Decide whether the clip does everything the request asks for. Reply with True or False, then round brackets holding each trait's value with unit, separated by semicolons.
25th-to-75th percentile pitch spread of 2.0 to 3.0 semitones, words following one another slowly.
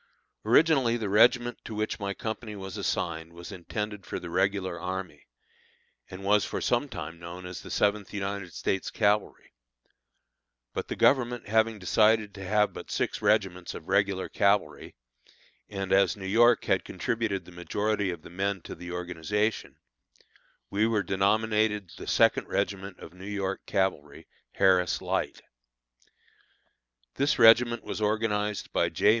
False (2.6 semitones; 150 wpm)